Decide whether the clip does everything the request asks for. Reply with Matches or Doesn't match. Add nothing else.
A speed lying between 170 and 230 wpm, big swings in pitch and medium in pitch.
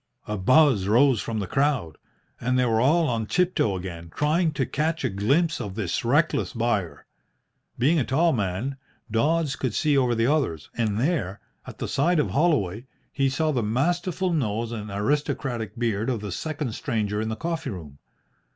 Doesn't match